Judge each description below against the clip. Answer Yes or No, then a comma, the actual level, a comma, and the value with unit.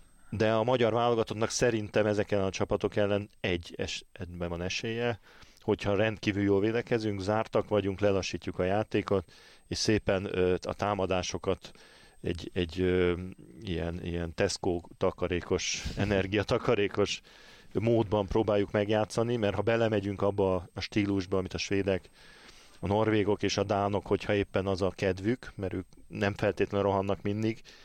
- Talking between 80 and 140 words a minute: Yes, average, 130 wpm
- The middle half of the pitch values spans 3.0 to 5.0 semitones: No, narrow, 2.4 semitones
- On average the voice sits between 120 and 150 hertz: No, low, 100 Hz